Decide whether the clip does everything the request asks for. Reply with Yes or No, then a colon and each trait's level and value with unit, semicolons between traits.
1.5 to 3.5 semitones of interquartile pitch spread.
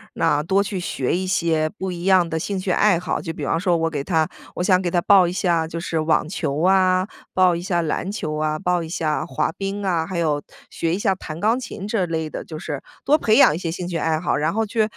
Yes: average, 2.8 semitones